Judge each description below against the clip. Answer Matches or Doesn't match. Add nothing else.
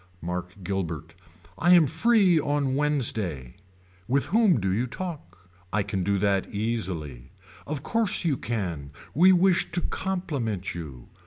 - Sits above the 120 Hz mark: Doesn't match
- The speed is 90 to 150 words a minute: Matches